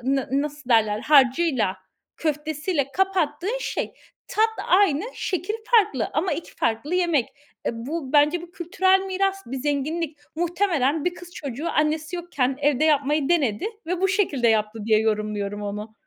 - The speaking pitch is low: No, very high, 300 Hz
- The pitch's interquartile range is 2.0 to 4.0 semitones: No, average, 5.3 semitones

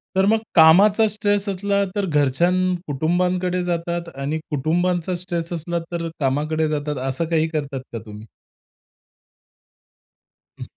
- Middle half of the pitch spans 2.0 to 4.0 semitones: Yes, average, 3.3 semitones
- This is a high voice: No, medium, 170 Hz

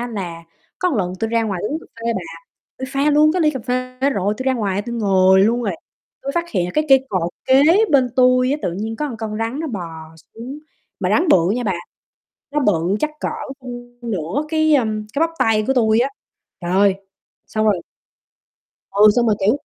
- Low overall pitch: No, high, 230 Hz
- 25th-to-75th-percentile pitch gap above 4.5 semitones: Yes, average, 5.1 semitones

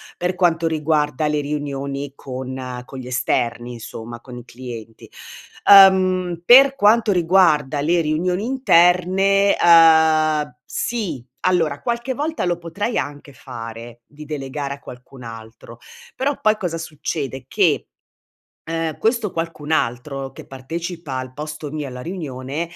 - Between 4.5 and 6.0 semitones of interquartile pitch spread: Yes, average, 5.1 semitones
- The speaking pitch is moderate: Yes, medium, 155 Hz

